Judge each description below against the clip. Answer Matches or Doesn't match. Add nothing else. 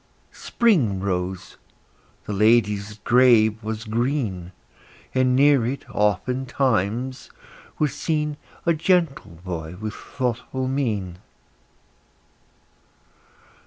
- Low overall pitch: Matches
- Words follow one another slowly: Matches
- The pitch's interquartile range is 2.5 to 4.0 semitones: Doesn't match